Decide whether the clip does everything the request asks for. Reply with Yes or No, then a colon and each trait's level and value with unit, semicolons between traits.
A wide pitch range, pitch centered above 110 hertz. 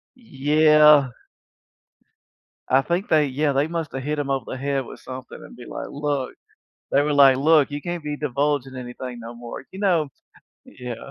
No: narrow, 2.6 semitones; medium, 140 Hz